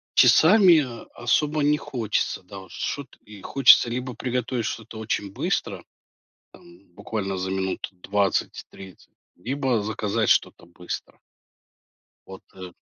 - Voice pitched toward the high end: No, low, 110 Hz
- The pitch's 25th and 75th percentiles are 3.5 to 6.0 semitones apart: Yes, average, 5.0 semitones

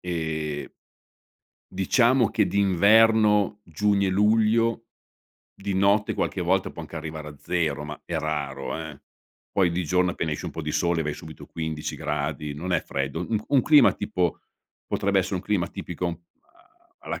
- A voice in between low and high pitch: No, very low, 90 Hz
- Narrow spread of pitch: No, average, 4.7 semitones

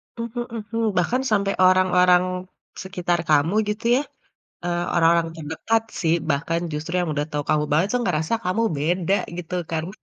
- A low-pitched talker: No, medium, 180 Hz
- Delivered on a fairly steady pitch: No, average, 3.9 semitones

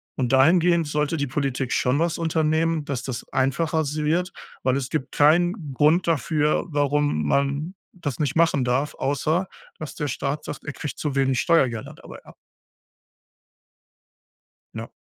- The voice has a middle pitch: Yes, medium, 145 Hz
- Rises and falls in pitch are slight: No, average, 3.0 semitones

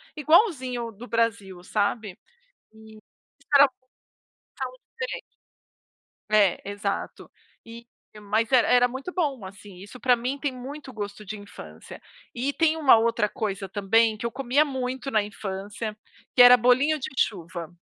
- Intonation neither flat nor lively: Yes, average, 4.2 semitones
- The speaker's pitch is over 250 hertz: No, high, 230 Hz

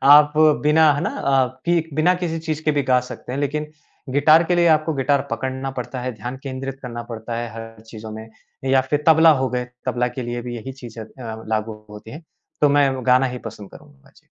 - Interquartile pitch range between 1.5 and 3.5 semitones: No, average, 4.2 semitones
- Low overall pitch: Yes, low, 130 Hz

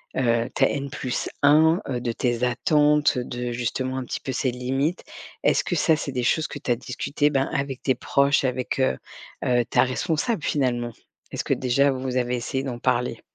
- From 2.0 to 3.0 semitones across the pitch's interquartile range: Yes, narrow, 2.4 semitones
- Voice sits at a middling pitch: No, low, 130 Hz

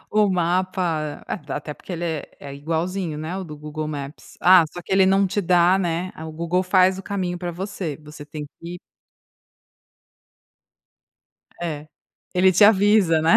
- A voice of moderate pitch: Yes, medium, 175 Hz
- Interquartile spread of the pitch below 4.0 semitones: Yes, average, 3.2 semitones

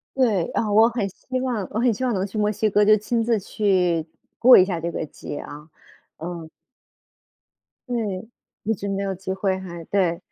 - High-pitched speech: Yes, high, 200 Hz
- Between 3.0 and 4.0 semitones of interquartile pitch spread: Yes, average, 3.4 semitones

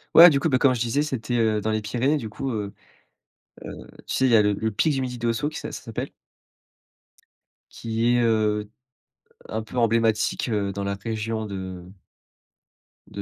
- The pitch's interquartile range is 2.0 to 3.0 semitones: Yes, average, 2.7 semitones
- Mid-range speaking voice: No, low, 115 Hz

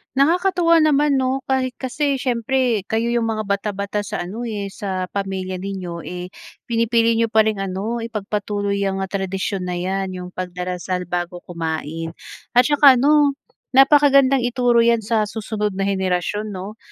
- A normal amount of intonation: Yes, average, 4.6 semitones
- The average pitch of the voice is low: No, high, 210 Hz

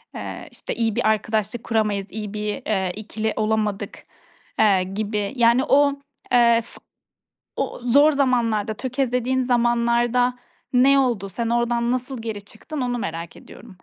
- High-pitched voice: Yes, high, 230 Hz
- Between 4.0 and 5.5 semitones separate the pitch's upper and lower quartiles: No, average, 2.7 semitones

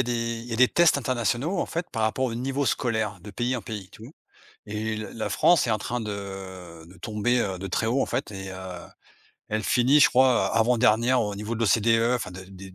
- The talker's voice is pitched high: No, low, 115 Hz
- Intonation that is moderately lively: Yes, average, 3.4 semitones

